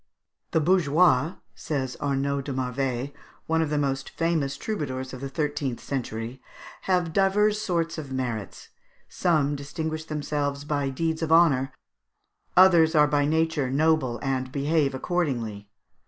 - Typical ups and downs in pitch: Yes, average, 3.4 semitones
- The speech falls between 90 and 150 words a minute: Yes, average, 140 wpm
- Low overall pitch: No, medium, 145 Hz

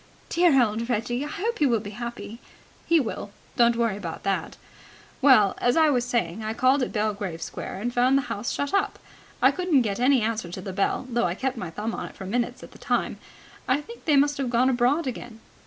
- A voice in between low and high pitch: No, high, 240 Hz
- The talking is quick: Yes, fast, 225 wpm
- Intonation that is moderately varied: Yes, average, 4.1 semitones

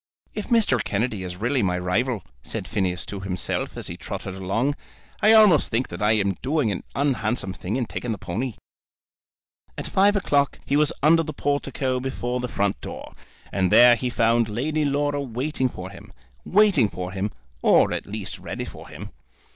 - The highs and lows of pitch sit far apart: Yes, wide, 6.3 semitones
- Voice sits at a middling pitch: No, low, 120 Hz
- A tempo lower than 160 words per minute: No, average, 180 wpm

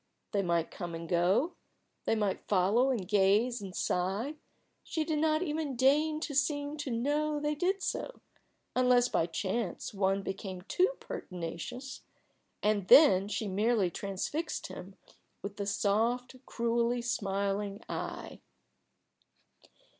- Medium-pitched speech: No, high, 225 Hz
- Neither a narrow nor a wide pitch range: No, wide, 6.5 semitones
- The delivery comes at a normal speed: No, slow, 130 wpm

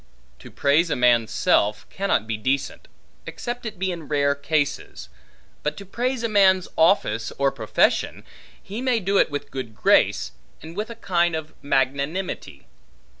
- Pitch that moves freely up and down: Yes, wide, 6.6 semitones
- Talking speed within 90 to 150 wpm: No, average, 160 wpm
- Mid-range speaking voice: Yes, medium, 160 Hz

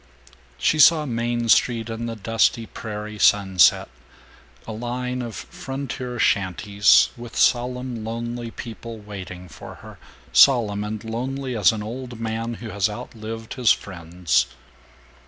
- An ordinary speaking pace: No, slow, 130 wpm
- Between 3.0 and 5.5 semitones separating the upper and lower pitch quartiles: No, narrow, 2.6 semitones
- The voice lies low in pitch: Yes, low, 115 Hz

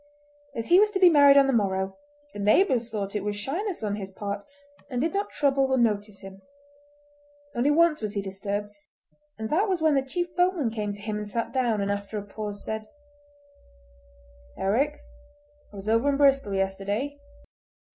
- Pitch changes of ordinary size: No, wide, 5.9 semitones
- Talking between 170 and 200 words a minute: Yes, average, 185 wpm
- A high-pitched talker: Yes, high, 225 Hz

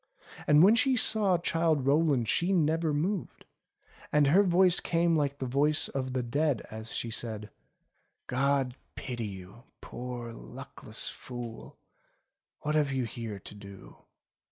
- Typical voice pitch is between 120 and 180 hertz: Yes, medium, 140 Hz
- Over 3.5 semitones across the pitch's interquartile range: Yes, wide, 5.6 semitones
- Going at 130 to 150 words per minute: Yes, average, 140 wpm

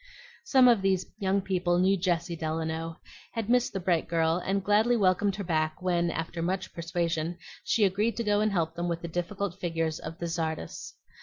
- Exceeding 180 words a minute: Yes, average, 190 wpm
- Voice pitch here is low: No, medium, 175 Hz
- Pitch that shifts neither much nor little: Yes, average, 3.1 semitones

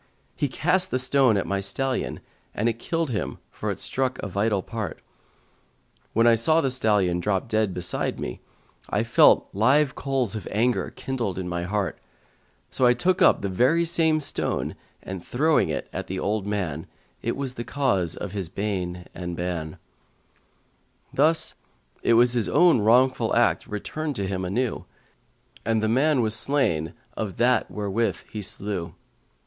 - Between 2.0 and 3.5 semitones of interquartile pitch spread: No, average, 5.3 semitones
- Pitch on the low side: Yes, low, 110 Hz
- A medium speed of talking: Yes, average, 160 wpm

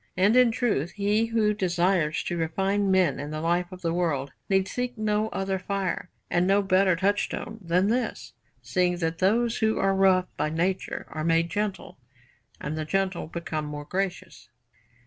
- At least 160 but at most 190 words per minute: Yes, average, 170 wpm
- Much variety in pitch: No, average, 3.4 semitones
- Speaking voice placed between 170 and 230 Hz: Yes, medium, 185 Hz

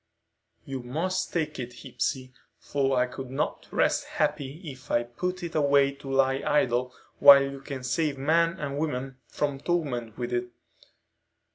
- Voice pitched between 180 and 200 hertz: No, low, 135 Hz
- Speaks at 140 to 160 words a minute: Yes, average, 155 wpm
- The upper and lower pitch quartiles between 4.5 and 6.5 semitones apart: No, average, 2.8 semitones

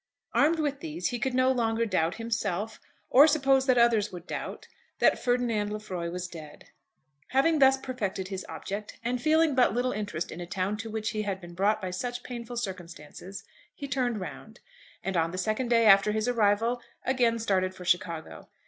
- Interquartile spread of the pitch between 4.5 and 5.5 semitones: Yes, average, 4.8 semitones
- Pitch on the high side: Yes, high, 220 Hz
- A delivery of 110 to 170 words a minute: No, average, 185 wpm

